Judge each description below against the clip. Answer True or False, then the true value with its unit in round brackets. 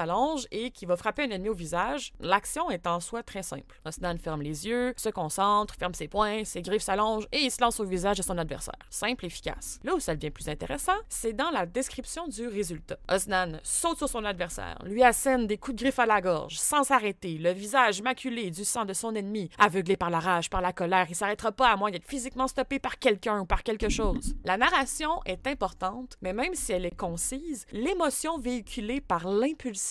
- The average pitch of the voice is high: True (210 Hz)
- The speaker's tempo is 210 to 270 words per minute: True (220 wpm)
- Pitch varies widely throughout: True (5.8 semitones)